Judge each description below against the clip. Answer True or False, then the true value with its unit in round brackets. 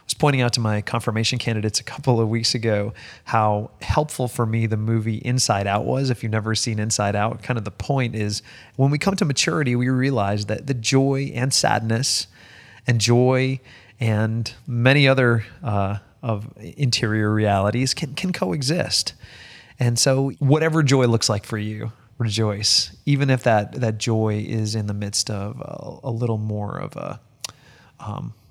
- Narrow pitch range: False (3.5 semitones)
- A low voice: True (115 Hz)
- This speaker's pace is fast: False (175 wpm)